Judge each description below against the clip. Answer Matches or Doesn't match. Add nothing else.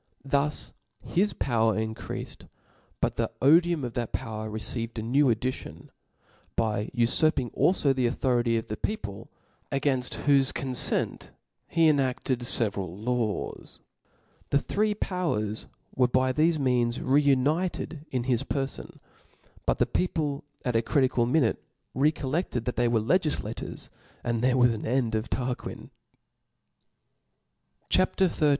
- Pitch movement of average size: Matches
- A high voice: Doesn't match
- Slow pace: Matches